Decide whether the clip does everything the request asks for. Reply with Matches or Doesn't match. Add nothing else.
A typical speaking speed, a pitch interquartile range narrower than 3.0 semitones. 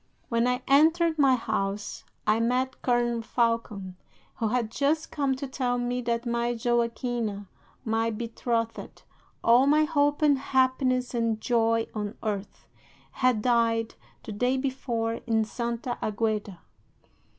Doesn't match